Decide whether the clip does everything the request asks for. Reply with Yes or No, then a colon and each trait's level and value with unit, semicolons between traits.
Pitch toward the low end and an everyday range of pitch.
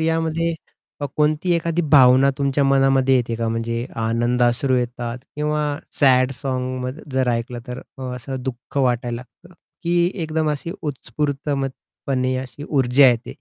Yes: low, 130 Hz; average, 3.3 semitones